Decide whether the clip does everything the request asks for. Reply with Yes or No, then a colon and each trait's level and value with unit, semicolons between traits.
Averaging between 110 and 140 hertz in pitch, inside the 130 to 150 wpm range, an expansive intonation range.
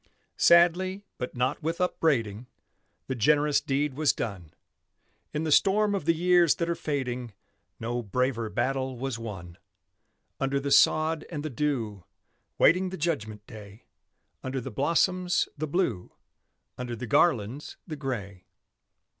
Yes: low, 135 Hz; average, 140 wpm; wide, 5.8 semitones